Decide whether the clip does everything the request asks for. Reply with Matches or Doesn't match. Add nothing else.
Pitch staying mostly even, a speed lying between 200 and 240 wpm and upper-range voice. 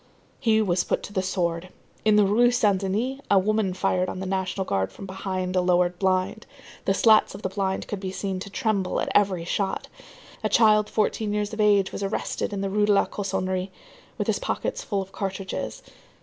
Matches